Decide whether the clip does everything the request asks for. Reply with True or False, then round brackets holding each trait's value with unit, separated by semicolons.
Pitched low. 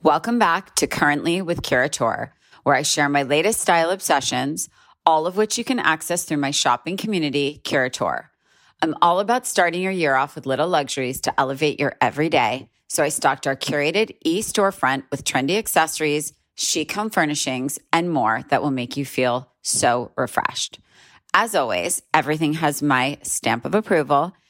False (150 Hz)